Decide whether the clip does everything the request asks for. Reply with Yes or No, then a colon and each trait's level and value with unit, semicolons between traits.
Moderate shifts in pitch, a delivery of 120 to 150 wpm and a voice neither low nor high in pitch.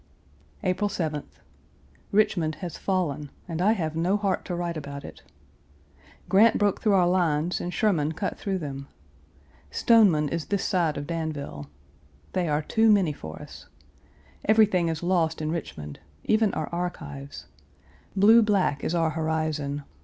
Yes: average, 4.2 semitones; average, 145 wpm; medium, 170 Hz